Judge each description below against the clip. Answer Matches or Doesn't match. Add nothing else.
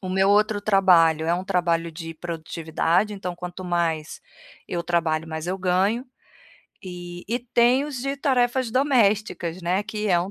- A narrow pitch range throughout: Doesn't match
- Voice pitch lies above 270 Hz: Doesn't match